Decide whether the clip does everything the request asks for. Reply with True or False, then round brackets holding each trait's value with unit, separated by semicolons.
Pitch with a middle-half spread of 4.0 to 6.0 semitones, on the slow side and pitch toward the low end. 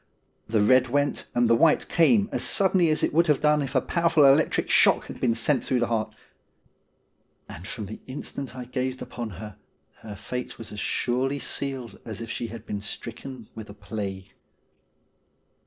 False (4.4 semitones; 185 wpm; 125 Hz)